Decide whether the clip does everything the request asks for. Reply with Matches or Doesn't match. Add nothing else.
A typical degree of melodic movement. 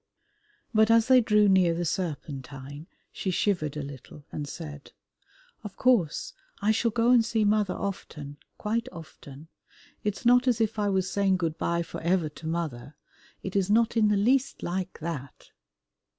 Doesn't match